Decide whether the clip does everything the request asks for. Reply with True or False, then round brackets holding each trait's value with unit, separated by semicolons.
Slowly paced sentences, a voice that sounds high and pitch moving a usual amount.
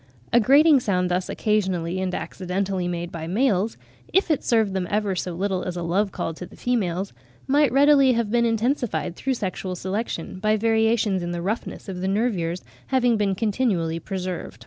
False (185 wpm; 195 Hz; 4.4 semitones)